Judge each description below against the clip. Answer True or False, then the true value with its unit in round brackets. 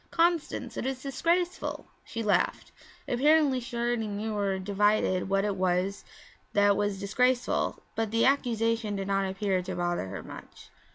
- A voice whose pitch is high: True (210 Hz)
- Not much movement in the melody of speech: False (4.1 semitones)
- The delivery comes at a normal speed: True (155 wpm)